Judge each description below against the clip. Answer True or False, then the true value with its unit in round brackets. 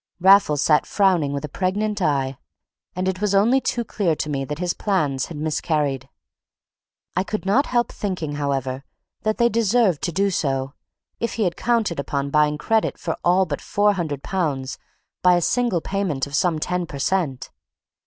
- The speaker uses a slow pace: False (175 wpm)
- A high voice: False (175 Hz)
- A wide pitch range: True (5.7 semitones)